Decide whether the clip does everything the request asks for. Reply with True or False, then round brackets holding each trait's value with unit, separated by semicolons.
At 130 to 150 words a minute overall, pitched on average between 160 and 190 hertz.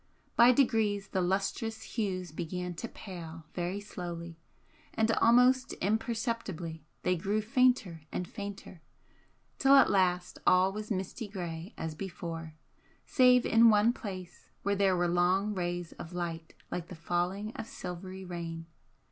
True (140 wpm; 185 Hz)